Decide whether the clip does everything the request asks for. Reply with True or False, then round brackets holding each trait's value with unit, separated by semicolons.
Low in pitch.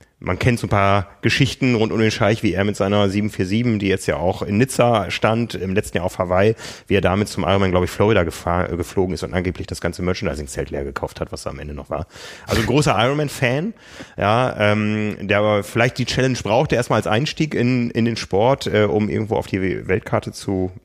True (105 Hz)